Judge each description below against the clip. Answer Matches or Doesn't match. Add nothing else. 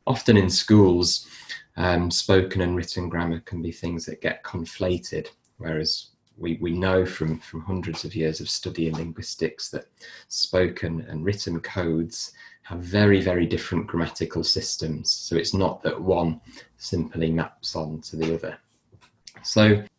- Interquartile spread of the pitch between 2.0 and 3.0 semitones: Matches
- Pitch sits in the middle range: Doesn't match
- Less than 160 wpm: Matches